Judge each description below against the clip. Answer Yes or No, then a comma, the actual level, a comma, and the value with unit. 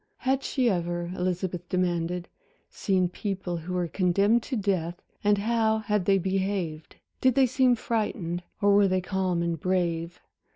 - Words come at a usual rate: Yes, average, 155 wpm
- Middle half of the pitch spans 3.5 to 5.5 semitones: No, average, 3.0 semitones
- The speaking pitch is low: No, medium, 185 Hz